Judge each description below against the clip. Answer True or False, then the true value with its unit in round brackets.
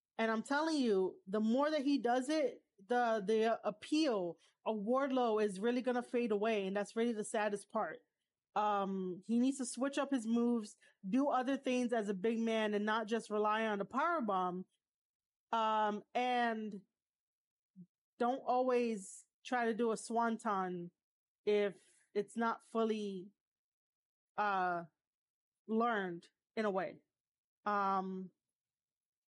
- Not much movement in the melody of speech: False (3.1 semitones)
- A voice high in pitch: True (220 Hz)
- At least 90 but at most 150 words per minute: True (140 wpm)